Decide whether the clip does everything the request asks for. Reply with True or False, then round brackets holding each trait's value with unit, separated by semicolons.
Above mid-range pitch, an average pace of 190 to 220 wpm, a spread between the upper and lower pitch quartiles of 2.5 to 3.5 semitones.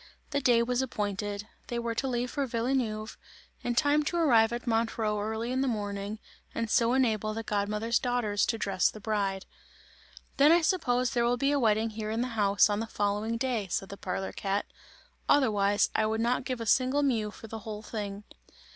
True (225 Hz; 200 wpm; 2.9 semitones)